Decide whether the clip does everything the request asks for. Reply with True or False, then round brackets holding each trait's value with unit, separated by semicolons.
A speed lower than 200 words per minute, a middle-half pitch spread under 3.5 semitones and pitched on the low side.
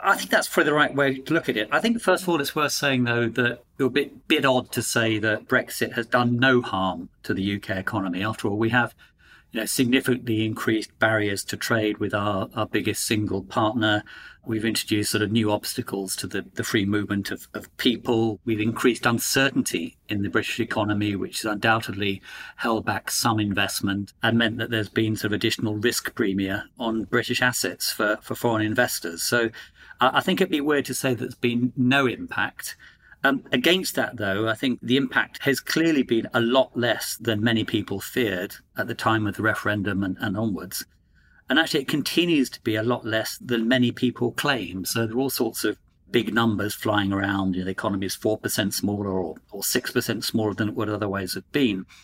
False (205 wpm; 3.1 semitones; 110 Hz)